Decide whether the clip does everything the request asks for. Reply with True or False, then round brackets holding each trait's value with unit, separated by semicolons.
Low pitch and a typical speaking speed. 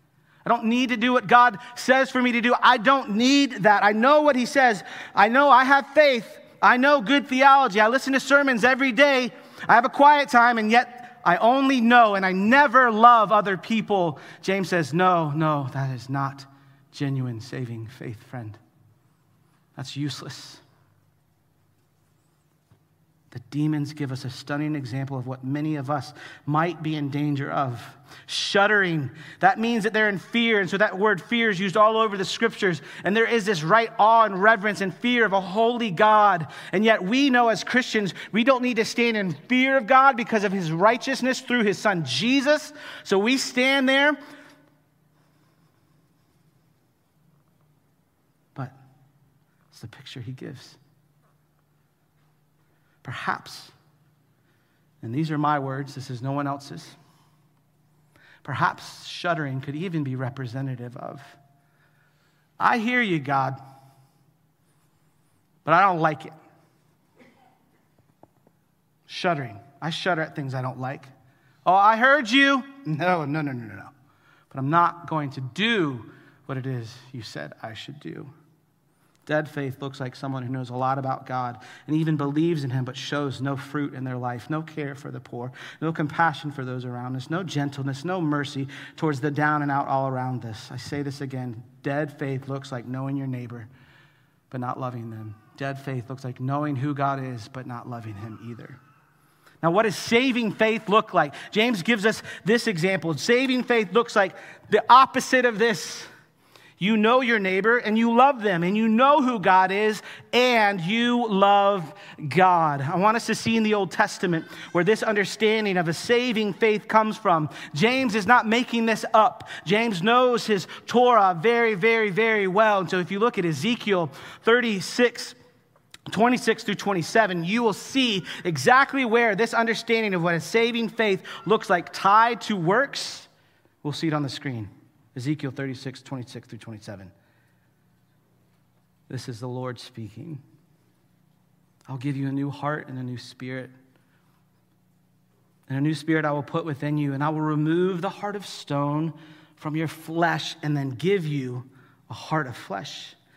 False (160 Hz; 170 wpm)